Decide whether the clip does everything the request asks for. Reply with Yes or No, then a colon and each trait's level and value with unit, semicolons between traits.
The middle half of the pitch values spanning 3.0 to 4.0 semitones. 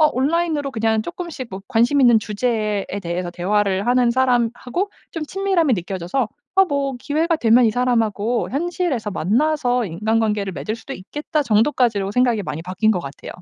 No: average, 5.3 semitones